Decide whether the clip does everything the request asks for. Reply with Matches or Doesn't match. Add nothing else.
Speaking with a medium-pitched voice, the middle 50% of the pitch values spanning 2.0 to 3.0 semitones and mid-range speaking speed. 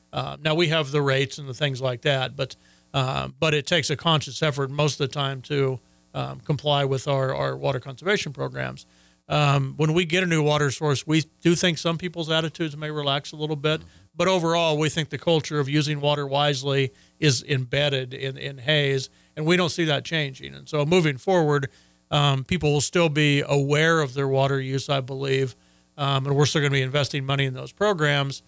Doesn't match